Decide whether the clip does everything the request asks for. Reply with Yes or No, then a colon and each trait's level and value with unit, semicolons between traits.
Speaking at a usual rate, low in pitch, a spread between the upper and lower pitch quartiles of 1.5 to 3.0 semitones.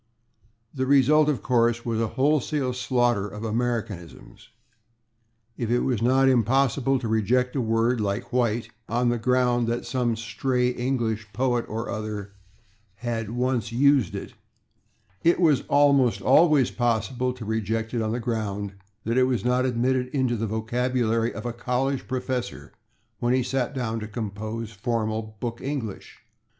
Yes: average, 150 wpm; low, 120 Hz; narrow, 2.4 semitones